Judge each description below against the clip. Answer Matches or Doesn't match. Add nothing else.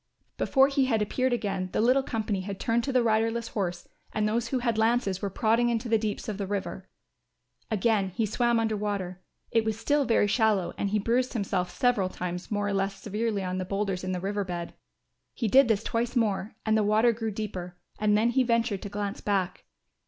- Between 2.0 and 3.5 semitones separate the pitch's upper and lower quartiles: Matches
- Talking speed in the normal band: Doesn't match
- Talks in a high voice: Matches